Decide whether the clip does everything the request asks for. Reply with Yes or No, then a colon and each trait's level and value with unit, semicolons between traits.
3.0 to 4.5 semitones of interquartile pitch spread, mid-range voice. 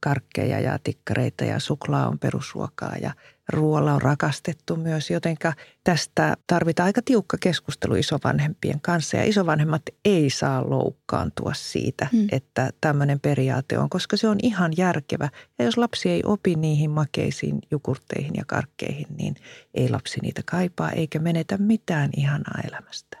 Yes: average, 3.8 semitones; medium, 160 Hz